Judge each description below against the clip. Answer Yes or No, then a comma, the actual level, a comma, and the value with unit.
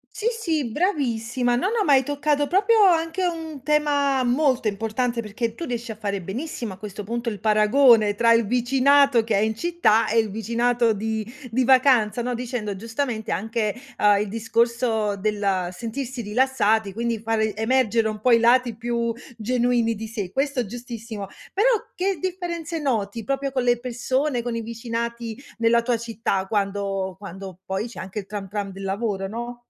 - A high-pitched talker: Yes, high, 235 Hz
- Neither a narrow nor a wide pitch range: Yes, average, 3.5 semitones